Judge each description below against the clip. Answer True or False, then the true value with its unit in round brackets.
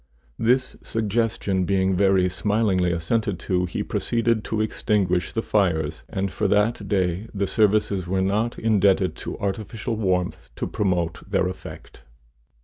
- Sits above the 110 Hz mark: False (100 Hz)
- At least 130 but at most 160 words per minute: True (140 wpm)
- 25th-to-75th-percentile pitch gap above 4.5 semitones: False (2.9 semitones)